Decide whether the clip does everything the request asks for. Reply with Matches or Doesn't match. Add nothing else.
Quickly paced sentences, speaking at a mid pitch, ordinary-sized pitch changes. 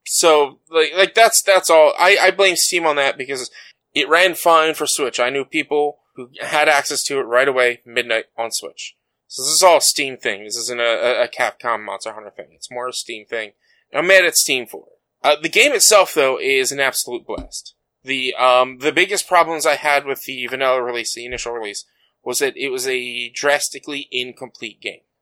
Doesn't match